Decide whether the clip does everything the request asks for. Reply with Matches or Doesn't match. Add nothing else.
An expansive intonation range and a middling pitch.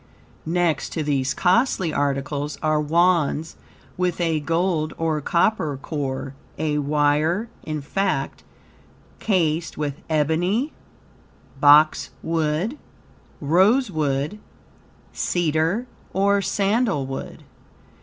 Doesn't match